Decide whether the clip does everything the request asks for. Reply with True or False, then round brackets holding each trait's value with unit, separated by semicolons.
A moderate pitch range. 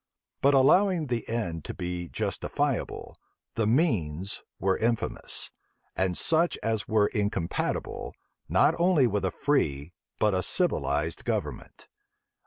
False (7.2 semitones)